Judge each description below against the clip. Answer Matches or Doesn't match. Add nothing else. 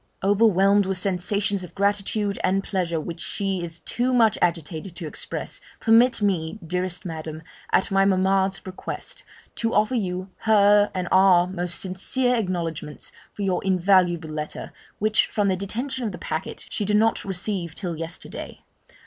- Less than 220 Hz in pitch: Matches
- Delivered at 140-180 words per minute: Matches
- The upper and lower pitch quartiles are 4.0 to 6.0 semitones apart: Doesn't match